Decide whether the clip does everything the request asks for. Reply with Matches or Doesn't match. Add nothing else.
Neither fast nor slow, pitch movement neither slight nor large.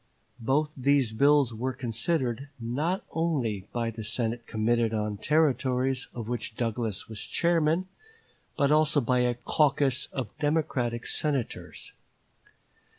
Doesn't match